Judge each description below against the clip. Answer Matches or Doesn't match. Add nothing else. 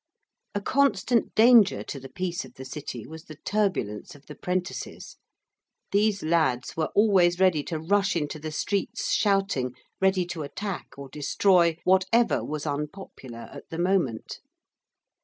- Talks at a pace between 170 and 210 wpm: Doesn't match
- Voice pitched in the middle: Matches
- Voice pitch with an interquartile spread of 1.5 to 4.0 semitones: Doesn't match